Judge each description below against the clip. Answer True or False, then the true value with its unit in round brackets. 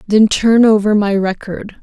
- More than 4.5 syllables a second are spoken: False (4.1 syllables/s)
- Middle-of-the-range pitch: False (210 Hz)